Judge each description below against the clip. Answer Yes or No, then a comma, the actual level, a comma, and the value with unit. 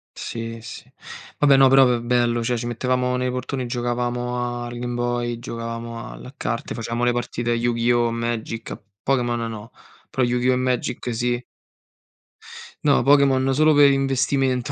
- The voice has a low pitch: Yes, low, 120 Hz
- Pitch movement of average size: No, narrow, 1.4 semitones